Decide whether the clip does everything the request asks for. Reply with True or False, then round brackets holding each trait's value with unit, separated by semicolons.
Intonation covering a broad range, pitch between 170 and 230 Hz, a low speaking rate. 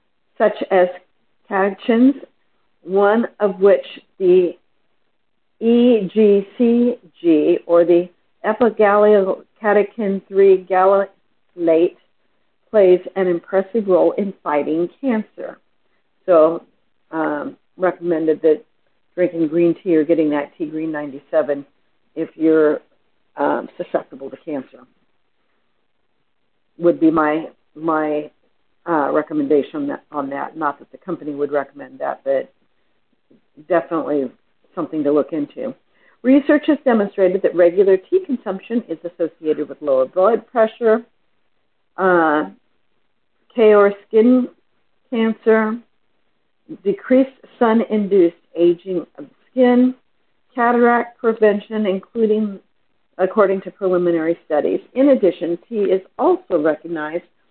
True (5.8 semitones; 190 Hz; 100 wpm)